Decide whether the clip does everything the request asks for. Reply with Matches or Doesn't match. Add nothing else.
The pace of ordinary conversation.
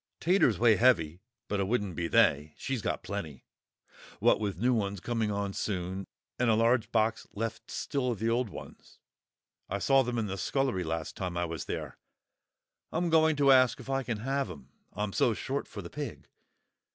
Matches